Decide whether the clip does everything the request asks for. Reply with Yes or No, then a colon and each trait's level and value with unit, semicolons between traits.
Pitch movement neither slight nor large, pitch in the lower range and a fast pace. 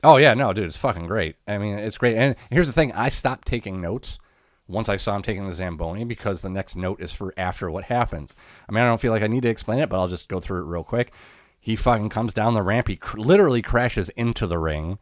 Yes: average, 4.4 semitones; low, 105 Hz; fast, 270 wpm